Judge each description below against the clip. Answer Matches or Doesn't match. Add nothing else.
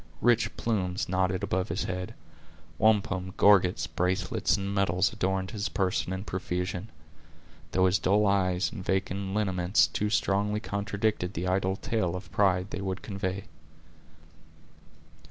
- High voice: Doesn't match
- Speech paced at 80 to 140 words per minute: Matches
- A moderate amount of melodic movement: Doesn't match